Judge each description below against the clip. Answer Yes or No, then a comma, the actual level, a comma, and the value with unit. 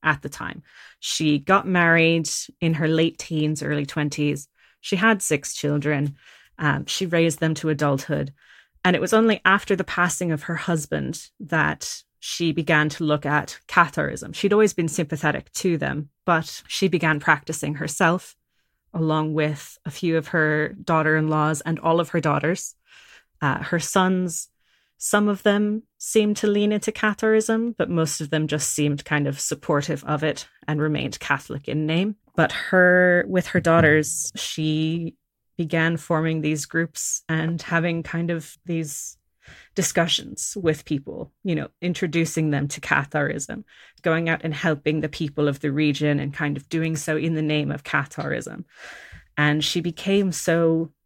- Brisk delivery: No, average, 160 wpm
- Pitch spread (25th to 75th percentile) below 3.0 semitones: Yes, narrow, 2.6 semitones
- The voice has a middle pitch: Yes, medium, 160 Hz